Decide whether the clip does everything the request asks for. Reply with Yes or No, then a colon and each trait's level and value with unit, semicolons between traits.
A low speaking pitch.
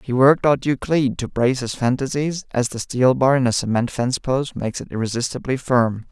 Yes: low, 130 Hz